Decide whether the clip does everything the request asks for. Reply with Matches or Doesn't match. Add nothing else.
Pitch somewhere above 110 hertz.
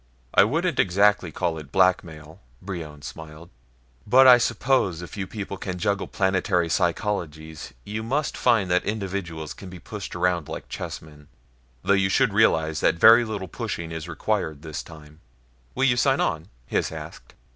Doesn't match